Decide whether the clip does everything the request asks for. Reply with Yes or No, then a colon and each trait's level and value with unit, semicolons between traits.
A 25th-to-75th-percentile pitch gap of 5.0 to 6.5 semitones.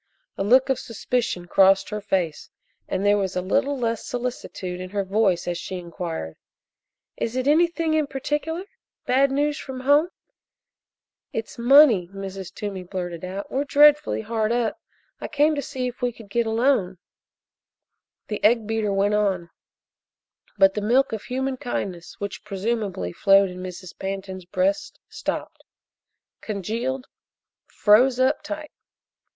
Yes: wide, 5.4 semitones